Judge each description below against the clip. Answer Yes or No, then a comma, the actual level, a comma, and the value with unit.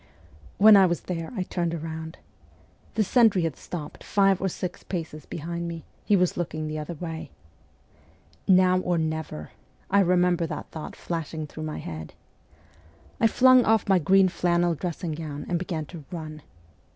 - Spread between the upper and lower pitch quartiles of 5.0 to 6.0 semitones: No, narrow, 2.6 semitones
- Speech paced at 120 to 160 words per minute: No, average, 170 wpm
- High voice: No, medium, 170 Hz